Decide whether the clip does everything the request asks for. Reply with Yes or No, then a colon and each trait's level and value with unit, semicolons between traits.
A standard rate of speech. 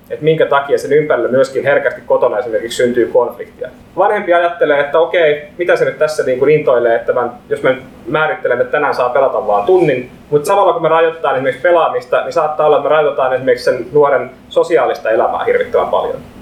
No: fast, 195 wpm